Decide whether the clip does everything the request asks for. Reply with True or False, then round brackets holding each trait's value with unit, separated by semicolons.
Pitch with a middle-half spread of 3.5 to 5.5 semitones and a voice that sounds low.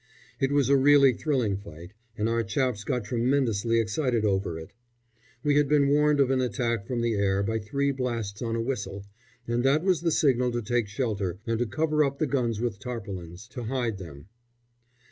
True (4.7 semitones; 120 Hz)